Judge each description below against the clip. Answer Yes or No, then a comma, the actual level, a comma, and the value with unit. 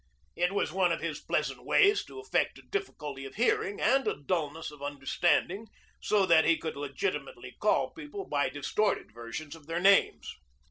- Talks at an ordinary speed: Yes, average, 175 wpm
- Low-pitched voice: No, medium, 170 Hz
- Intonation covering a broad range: Yes, wide, 6.6 semitones